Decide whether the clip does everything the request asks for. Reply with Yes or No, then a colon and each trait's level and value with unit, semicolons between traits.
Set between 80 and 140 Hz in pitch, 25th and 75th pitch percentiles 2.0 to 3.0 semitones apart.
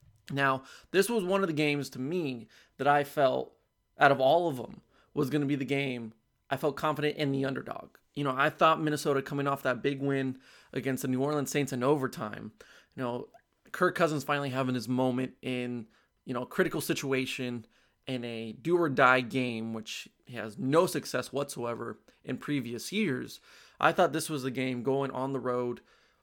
Yes: low, 135 Hz; narrow, 2.6 semitones